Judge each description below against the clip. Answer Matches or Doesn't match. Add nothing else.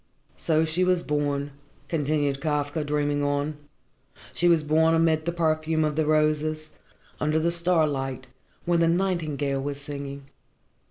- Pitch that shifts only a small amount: Matches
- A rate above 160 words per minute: Doesn't match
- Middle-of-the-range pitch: Matches